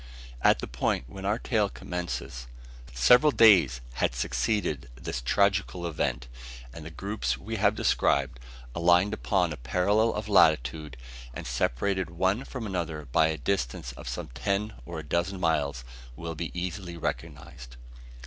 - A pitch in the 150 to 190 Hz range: No, very low, 85 Hz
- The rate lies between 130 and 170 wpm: Yes, average, 150 wpm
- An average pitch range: No, wide, 7.0 semitones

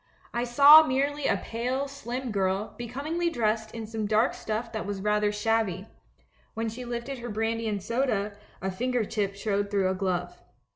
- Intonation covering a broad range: No, average, 3.3 semitones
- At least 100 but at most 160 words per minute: No, average, 175 wpm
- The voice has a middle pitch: No, high, 225 Hz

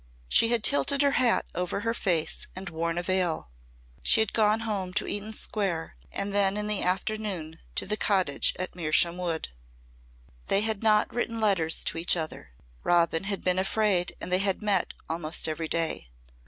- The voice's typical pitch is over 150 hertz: Yes, high, 190 Hz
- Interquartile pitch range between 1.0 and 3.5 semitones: No, average, 4.0 semitones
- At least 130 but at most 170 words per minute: No, average, 180 wpm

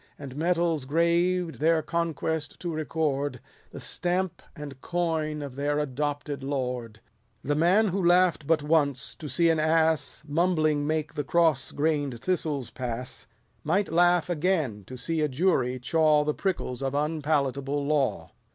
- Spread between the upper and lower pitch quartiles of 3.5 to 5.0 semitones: No, average, 3.1 semitones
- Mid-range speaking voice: Yes, medium, 155 Hz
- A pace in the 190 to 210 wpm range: No, average, 150 wpm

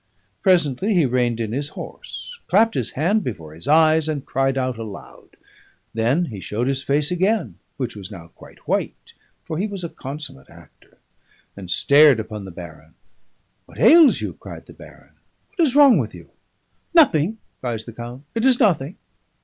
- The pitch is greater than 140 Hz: No, low, 135 Hz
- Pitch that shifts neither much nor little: No, wide, 8.1 semitones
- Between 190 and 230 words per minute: No, average, 175 wpm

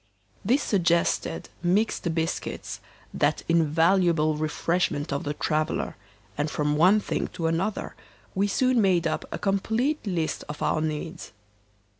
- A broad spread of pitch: No, average, 3.9 semitones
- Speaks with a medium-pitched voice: Yes, medium, 170 Hz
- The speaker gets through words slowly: Yes, slow, 130 wpm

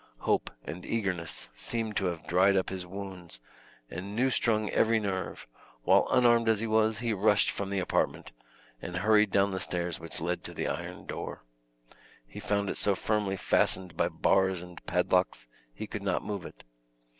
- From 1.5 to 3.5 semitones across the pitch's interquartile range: Yes, average, 3.1 semitones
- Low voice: Yes, very low, 95 Hz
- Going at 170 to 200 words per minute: Yes, average, 180 wpm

